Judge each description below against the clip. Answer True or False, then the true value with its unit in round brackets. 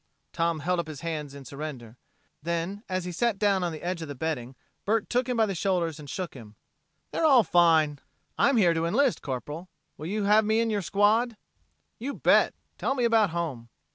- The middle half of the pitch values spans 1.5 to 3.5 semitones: False (5.6 semitones)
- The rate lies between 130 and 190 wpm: False (205 wpm)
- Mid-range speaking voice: True (175 Hz)